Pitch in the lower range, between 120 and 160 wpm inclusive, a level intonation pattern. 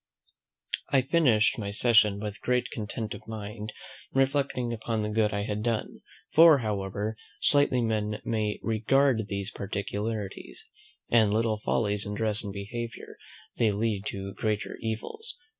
Yes: low, 110 Hz; average, 140 wpm; narrow, 2.2 semitones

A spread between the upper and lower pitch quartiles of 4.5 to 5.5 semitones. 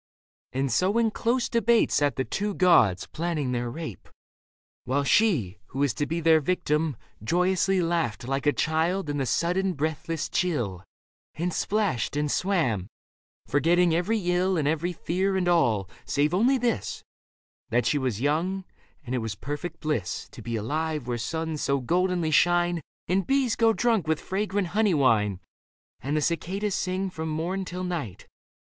Yes: average, 5.0 semitones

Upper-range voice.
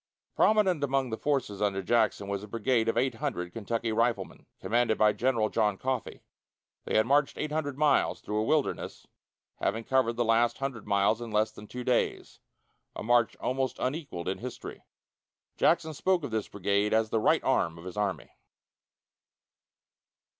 No: low, 115 Hz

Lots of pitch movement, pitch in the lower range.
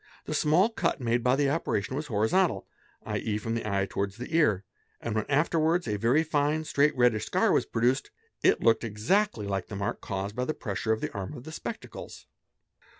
Yes: wide, 6.4 semitones; low, 120 Hz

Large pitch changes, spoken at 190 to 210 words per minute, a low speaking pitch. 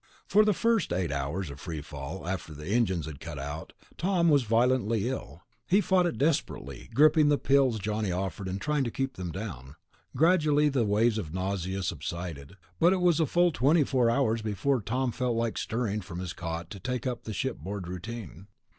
Yes: wide, 7.6 semitones; average, 195 wpm; low, 110 Hz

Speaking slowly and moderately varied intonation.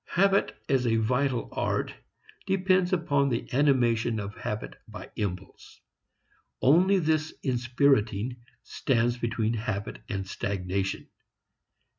Yes: slow, 105 wpm; average, 5.0 semitones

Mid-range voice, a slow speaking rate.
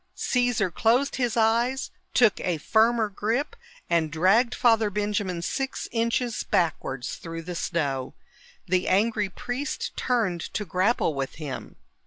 No: high, 210 Hz; slow, 130 wpm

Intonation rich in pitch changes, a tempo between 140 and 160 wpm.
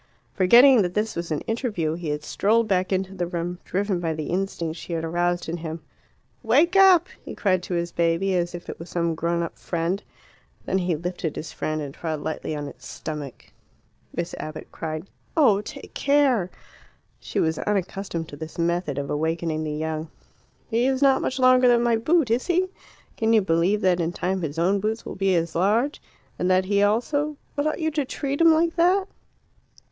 No: wide, 5.8 semitones; average, 200 wpm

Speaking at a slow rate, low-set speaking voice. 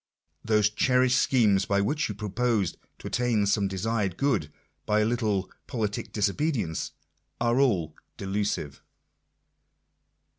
Yes: slow, 115 wpm; low, 105 Hz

